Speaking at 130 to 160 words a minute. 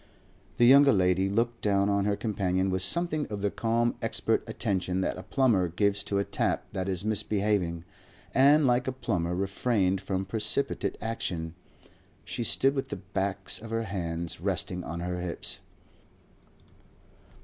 Yes: average, 155 wpm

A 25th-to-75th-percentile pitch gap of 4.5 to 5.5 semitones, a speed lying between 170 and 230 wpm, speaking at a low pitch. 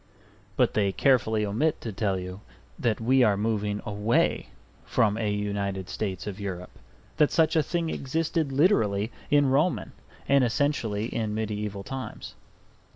No: average, 4.9 semitones; average, 145 wpm; low, 110 Hz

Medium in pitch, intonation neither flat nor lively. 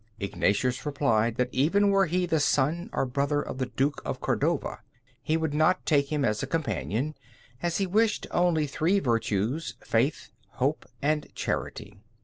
Yes: medium, 145 Hz; average, 4.8 semitones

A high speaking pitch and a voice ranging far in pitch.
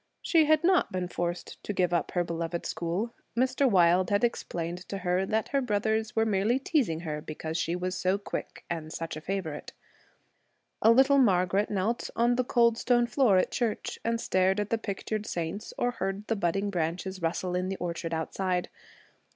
No: high, 195 Hz; average, 4.8 semitones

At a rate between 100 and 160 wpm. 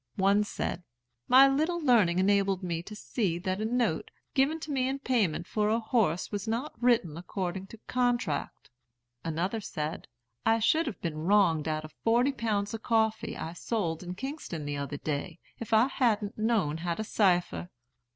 No: average, 175 wpm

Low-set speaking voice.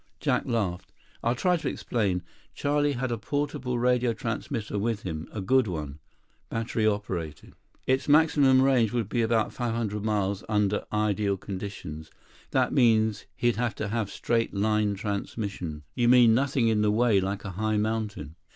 Yes: low, 110 Hz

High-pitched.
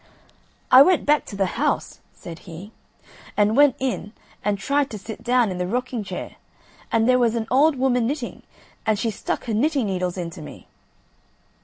Yes: high, 230 Hz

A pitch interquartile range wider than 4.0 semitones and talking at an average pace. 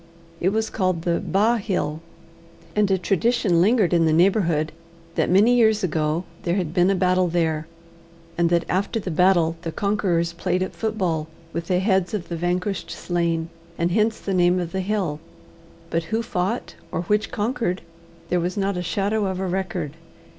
No: average, 3.0 semitones; average, 180 wpm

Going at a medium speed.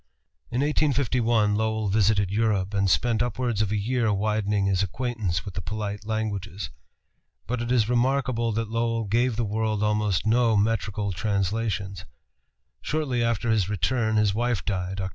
Yes: average, 155 wpm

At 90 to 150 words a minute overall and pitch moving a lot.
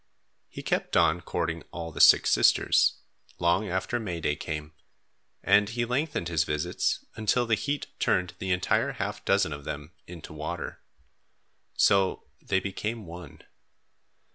No: average, 140 wpm; average, 4.7 semitones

